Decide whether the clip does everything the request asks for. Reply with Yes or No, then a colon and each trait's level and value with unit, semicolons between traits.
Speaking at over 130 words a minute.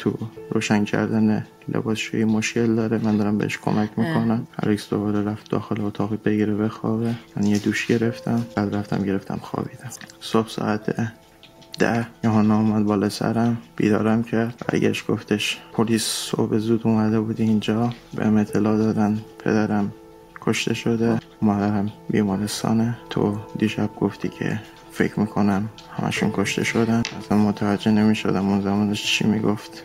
Yes: average, 140 wpm